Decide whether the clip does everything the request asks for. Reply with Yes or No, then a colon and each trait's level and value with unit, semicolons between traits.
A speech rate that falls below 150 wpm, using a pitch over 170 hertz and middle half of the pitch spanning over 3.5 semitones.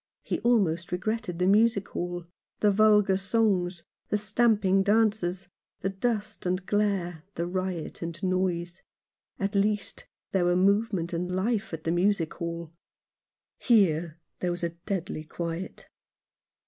No: slow, 135 wpm; medium, 185 Hz; average, 3.1 semitones